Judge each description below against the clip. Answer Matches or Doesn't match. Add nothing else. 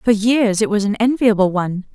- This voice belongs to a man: Doesn't match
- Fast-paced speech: Matches